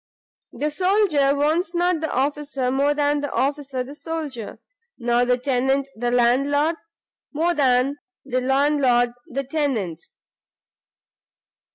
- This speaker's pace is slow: Yes, slow, 120 wpm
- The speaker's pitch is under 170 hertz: No, very high, 280 Hz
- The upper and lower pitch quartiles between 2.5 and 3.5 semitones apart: Yes, average, 2.8 semitones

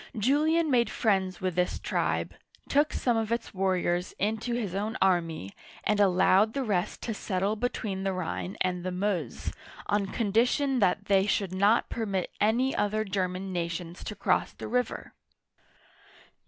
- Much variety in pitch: No, average, 3.4 semitones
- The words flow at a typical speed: Yes, average, 155 wpm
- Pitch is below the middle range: No, high, 200 Hz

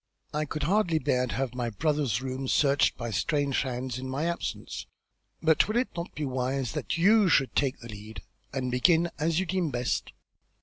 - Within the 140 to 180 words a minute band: No, average, 190 wpm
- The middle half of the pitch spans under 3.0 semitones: No, average, 4.6 semitones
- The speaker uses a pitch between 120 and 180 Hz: Yes, medium, 140 Hz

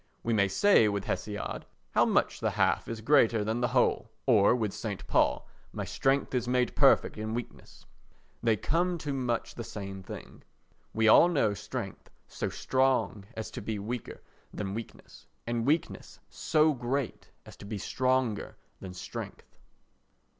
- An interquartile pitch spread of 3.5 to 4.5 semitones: Yes, average, 3.8 semitones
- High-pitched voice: No, low, 115 Hz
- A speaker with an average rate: Yes, average, 160 wpm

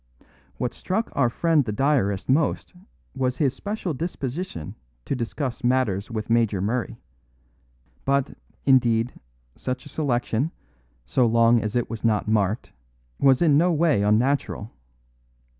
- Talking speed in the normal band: No, slow, 130 wpm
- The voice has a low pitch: Yes, low, 125 Hz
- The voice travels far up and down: No, average, 4.0 semitones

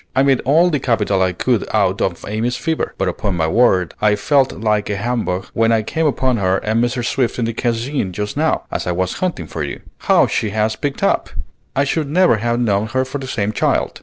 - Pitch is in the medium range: No, low, 115 Hz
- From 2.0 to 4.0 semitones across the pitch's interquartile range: No, average, 4.5 semitones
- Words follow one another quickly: Yes, fast, 230 wpm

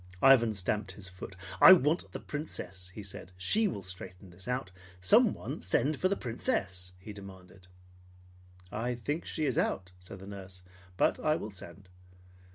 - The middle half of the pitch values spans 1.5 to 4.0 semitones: No, average, 5.3 semitones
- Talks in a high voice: No, low, 100 Hz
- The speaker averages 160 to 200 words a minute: Yes, average, 165 wpm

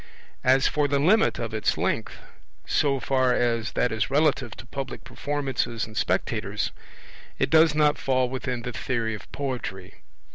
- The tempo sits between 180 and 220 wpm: No, average, 155 wpm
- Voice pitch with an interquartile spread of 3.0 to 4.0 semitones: Yes, average, 3.5 semitones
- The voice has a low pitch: Yes, low, 130 Hz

